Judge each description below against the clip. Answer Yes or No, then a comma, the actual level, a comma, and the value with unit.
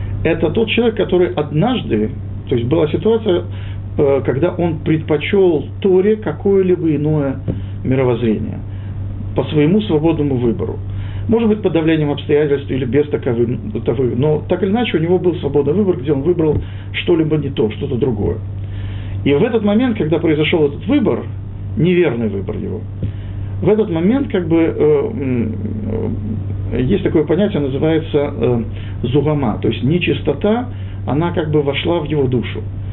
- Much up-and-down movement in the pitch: Yes, wide, 8.2 semitones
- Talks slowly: No, average, 140 wpm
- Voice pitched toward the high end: No, low, 135 Hz